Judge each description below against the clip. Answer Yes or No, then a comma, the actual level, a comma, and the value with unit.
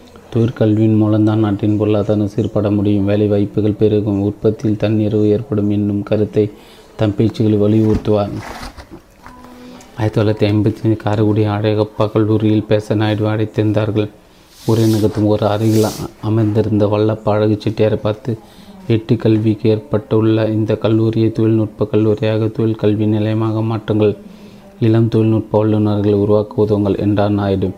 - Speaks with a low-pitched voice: Yes, low, 105 Hz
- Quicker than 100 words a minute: Yes, average, 110 wpm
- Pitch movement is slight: Yes, narrow, 0.8 semitones